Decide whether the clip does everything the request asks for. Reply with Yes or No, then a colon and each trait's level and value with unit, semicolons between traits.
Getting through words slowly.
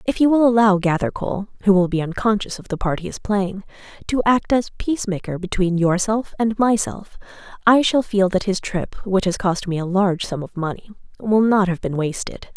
No: fast, 205 wpm